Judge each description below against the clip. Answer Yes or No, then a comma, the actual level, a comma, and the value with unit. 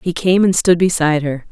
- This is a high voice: No, medium, 170 Hz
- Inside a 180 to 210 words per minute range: No, fast, 240 wpm